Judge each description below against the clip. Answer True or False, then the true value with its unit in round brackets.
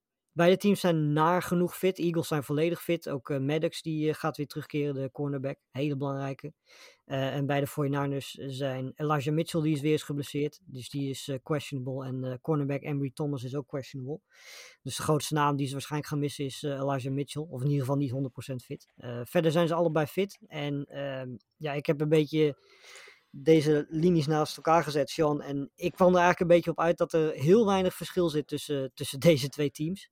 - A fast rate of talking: True (210 wpm)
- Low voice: False (150 Hz)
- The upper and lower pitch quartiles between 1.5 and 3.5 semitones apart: True (2.8 semitones)